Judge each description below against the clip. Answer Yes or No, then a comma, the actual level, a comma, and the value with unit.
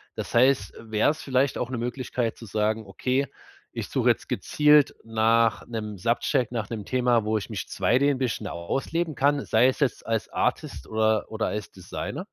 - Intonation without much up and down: No, average, 3.2 semitones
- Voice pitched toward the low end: Yes, low, 115 Hz